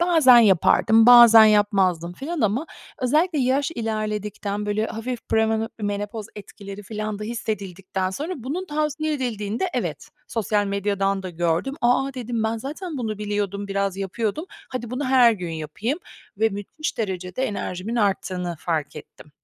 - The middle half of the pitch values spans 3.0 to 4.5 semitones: Yes, average, 4.1 semitones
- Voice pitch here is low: No, high, 215 Hz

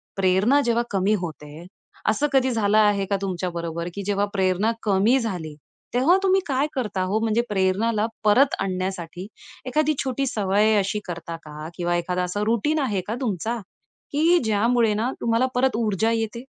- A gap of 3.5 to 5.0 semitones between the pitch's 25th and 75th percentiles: Yes, average, 4.2 semitones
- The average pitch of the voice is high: Yes, high, 210 Hz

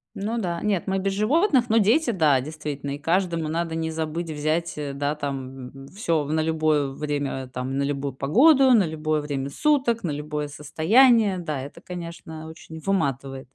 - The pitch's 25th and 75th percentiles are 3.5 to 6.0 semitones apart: Yes, average, 5.1 semitones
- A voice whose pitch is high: No, medium, 160 Hz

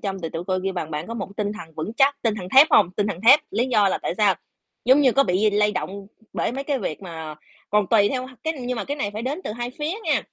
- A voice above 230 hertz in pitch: No, high, 210 Hz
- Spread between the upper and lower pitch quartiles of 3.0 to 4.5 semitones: No, average, 5.1 semitones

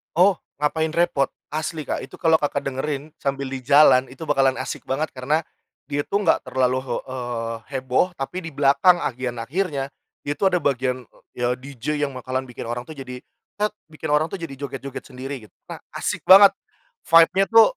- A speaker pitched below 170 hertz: Yes, medium, 140 Hz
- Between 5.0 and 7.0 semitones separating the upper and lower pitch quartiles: No, average, 3.6 semitones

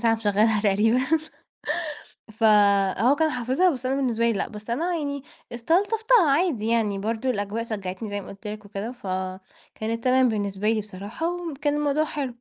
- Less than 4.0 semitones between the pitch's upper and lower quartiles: No, average, 5.2 semitones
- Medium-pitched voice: No, high, 230 Hz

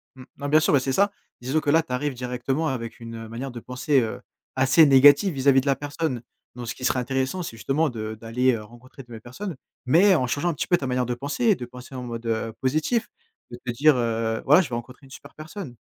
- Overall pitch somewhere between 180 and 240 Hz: No, low, 130 Hz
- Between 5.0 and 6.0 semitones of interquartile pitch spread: No, average, 3.6 semitones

